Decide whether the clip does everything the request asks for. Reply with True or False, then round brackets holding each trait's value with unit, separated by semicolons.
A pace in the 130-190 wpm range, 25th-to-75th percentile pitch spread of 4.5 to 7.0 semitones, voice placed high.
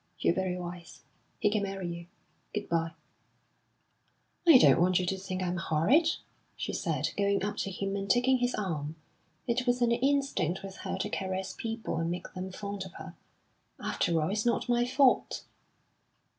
True (175 wpm; 4.9 semitones; 195 Hz)